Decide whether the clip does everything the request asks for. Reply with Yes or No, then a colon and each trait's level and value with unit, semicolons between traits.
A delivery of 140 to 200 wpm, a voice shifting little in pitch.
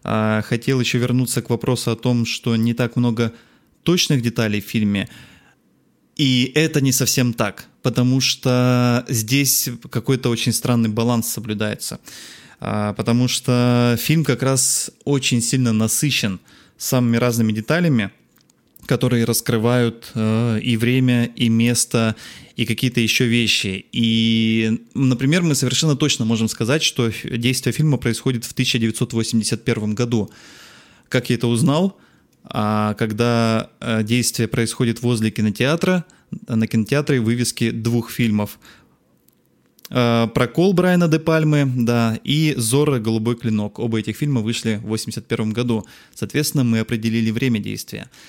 No: average, 125 wpm; narrow, 2.2 semitones